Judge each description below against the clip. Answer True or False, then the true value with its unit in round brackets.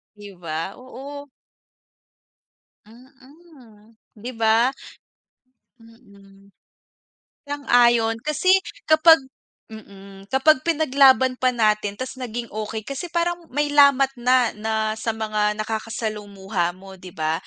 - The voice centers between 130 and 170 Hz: False (230 Hz)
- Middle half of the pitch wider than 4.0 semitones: True (4.4 semitones)